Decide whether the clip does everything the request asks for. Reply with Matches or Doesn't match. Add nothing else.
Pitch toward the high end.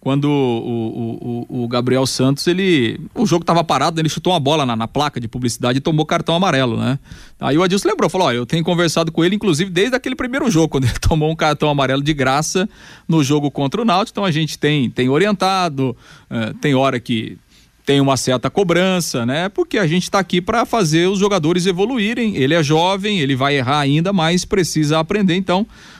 Doesn't match